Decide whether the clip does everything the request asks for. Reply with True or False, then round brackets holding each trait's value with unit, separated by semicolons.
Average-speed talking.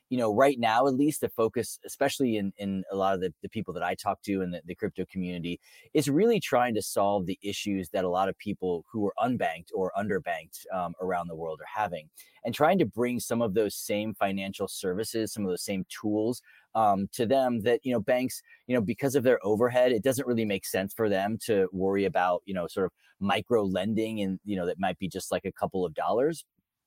False (235 wpm)